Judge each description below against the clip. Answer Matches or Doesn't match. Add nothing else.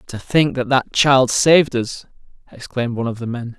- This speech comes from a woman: Doesn't match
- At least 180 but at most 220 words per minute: Matches